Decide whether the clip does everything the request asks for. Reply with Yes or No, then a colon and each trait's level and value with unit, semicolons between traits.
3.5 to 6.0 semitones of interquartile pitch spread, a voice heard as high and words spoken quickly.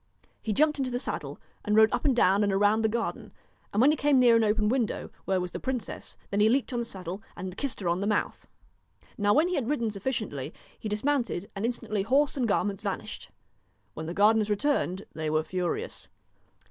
Yes: average, 4.2 semitones; high, 215 Hz; fast, 215 wpm